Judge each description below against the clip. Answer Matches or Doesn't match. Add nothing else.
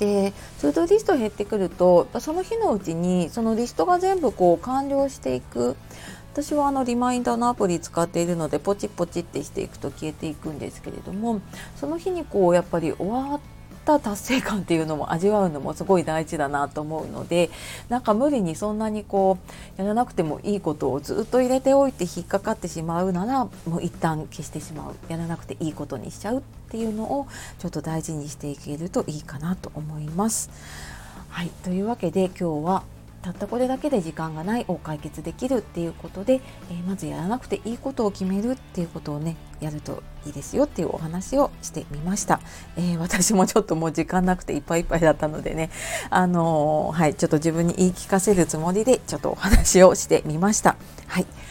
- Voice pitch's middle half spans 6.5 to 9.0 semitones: Doesn't match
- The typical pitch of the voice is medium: Matches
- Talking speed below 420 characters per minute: Doesn't match